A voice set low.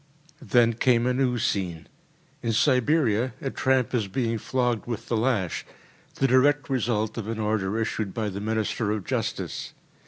Yes: low, 115 Hz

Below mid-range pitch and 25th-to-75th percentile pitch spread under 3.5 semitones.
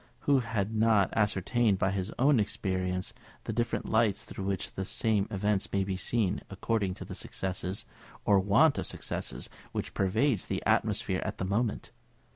Yes: low, 100 Hz; average, 2.9 semitones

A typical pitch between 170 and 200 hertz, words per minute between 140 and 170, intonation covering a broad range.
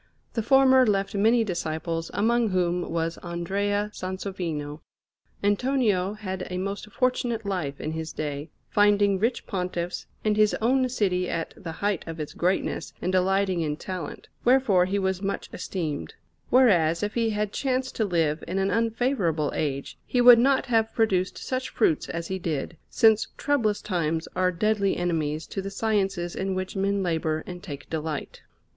No: high, 190 Hz; average, 165 wpm; average, 4.3 semitones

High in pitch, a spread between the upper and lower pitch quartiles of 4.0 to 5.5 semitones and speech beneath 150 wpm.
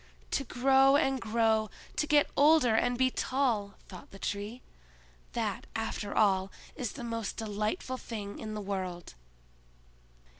Yes: high, 220 Hz; average, 4.3 semitones; slow, 135 wpm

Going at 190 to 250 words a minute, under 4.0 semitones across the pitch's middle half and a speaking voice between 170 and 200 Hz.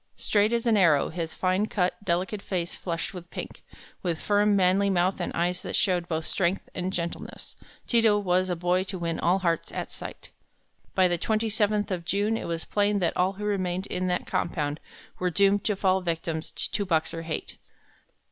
Yes: average, 195 wpm; average, 2.9 semitones; medium, 185 Hz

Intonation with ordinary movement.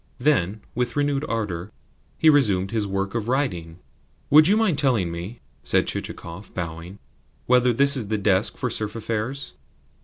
No: wide, 6.0 semitones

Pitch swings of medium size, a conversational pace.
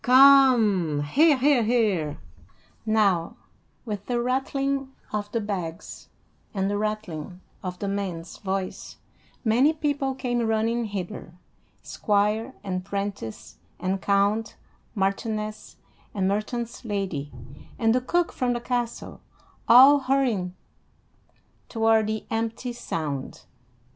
No: average, 4.1 semitones; slow, 110 wpm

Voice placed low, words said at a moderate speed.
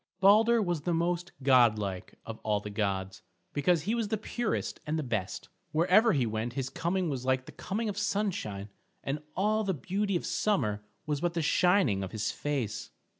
No: medium, 155 Hz; average, 185 wpm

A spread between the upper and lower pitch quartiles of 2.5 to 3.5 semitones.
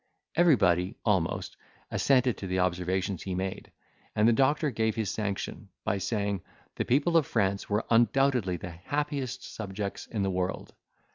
No: average, 5.2 semitones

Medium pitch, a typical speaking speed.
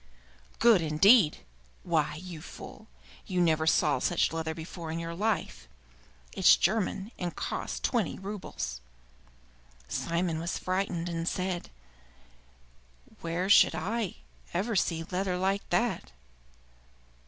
No: medium, 175 Hz; slow, 115 wpm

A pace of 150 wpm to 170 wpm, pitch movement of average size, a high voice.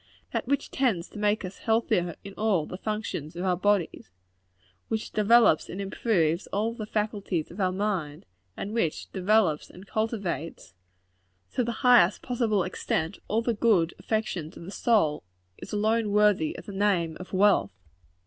Yes: average, 160 wpm; average, 4.0 semitones; high, 205 Hz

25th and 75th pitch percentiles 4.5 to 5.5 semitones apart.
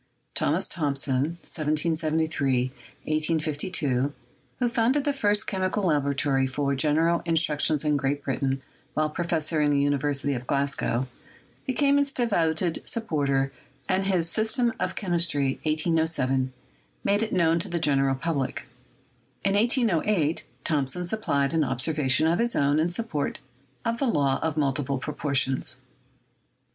No: average, 4.1 semitones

